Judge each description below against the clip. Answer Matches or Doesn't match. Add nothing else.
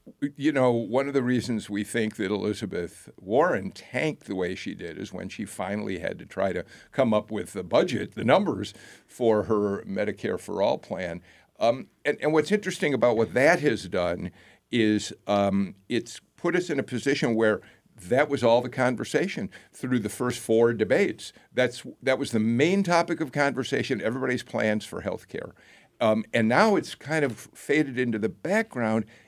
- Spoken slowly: Doesn't match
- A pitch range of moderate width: Matches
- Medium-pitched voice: Doesn't match